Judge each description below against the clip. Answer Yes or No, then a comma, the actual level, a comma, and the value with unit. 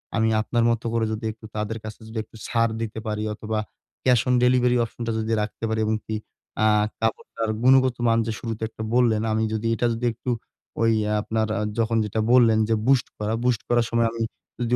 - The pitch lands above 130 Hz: No, low, 115 Hz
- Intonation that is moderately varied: No, narrow, 1.4 semitones